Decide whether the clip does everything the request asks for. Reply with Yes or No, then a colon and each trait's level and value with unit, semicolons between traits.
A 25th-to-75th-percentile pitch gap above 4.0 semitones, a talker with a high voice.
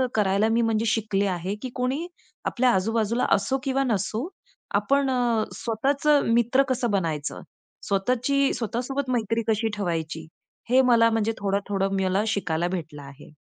Yes: average, 4.5 semitones; high, 225 Hz